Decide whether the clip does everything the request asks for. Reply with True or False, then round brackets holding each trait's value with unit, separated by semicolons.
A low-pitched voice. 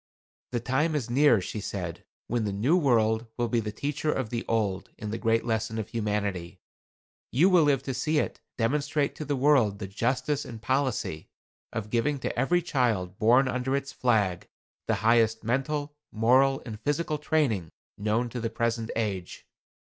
True (120 Hz)